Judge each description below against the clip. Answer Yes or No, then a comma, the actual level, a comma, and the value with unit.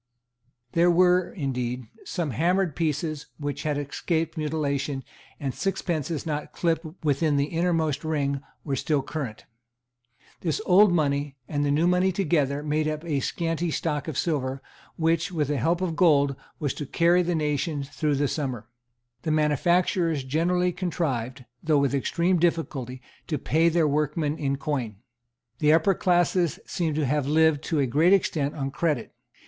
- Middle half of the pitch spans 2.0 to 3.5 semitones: Yes, average, 3.1 semitones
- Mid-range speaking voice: Yes, medium, 155 Hz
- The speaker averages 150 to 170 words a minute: Yes, average, 155 wpm